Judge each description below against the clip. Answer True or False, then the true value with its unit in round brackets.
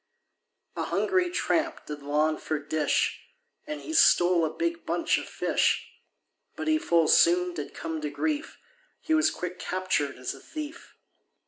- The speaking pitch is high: False (180 Hz)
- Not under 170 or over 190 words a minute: False (155 wpm)